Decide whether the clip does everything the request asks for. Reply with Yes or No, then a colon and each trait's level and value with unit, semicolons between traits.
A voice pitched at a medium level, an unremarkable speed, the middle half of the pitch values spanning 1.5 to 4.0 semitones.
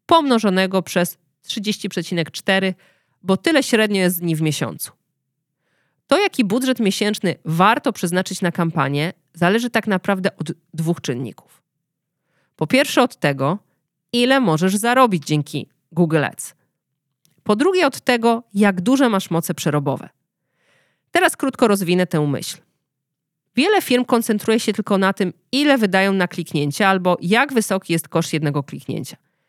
No: medium, 180 Hz; average, 135 wpm; wide, 5.6 semitones